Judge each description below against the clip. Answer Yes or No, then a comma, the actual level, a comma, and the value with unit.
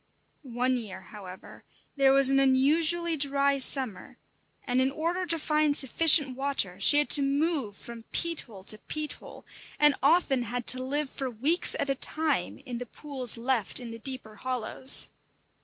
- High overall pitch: Yes, very high, 270 Hz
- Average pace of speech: Yes, average, 170 wpm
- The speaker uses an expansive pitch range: No, average, 3.4 semitones